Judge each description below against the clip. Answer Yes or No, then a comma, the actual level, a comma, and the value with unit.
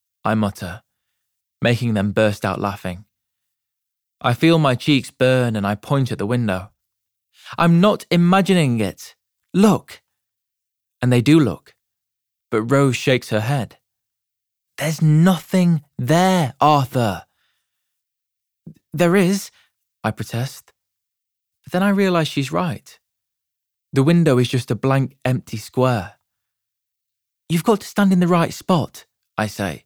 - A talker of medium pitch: No, low, 120 Hz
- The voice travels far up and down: Yes, wide, 6.3 semitones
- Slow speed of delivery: Yes, slow, 130 wpm